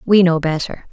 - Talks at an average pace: Yes, average, 195 wpm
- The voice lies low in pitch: No, medium, 170 Hz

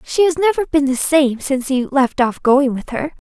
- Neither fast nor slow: No, fast, 235 wpm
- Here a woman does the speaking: Yes, female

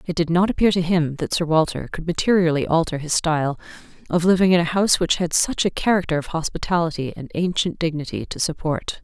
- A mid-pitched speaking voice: Yes, medium, 165 Hz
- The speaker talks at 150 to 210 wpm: Yes, fast, 205 wpm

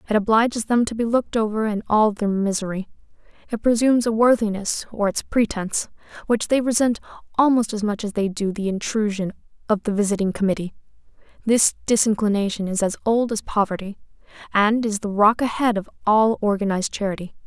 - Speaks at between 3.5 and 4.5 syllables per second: No, 5.8 syllables/s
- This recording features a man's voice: No, female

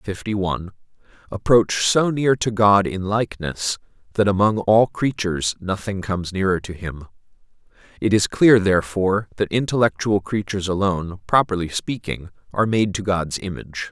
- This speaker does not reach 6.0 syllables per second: Yes, 5.2 syllables/s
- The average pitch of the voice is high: No, low, 100 Hz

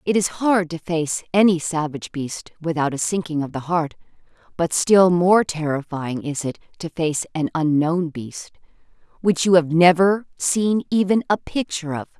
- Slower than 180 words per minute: Yes, average, 165 wpm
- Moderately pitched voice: Yes, medium, 170 Hz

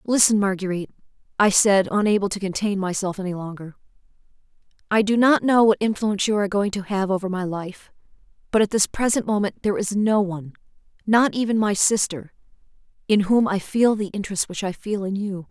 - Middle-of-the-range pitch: No, high, 200 Hz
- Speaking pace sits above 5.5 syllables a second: Yes, 5.9 syllables/s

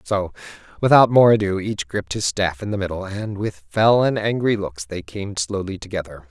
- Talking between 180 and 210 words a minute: Yes, average, 200 wpm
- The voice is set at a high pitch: No, low, 100 Hz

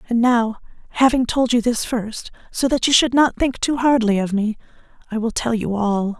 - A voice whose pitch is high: Yes, high, 235 Hz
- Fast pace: Yes, fast, 215 wpm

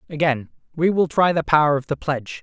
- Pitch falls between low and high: Yes, medium, 150 Hz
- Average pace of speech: No, fast, 220 wpm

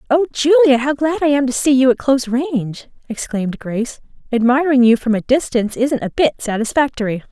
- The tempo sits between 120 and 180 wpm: No, average, 190 wpm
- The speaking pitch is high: Yes, very high, 260 Hz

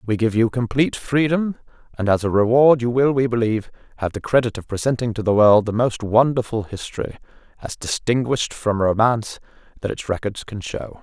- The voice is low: Yes, low, 115 Hz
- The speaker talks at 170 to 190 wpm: Yes, average, 185 wpm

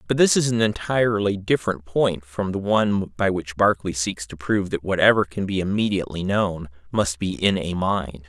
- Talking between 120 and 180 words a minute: No, average, 195 wpm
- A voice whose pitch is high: No, very low, 95 Hz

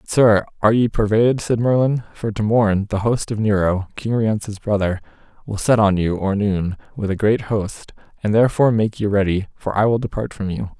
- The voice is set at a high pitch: No, low, 105 Hz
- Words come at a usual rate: No, fast, 210 wpm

